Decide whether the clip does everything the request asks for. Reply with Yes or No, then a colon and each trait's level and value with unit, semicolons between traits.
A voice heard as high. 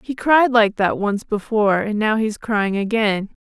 Yes: high, 215 Hz